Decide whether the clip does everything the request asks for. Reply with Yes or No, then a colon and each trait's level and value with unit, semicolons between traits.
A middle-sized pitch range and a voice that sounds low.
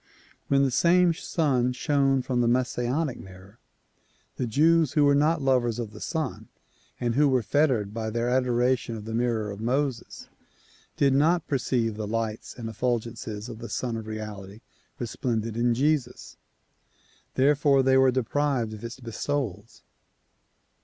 Yes: average, 3.6 semitones; low, 125 Hz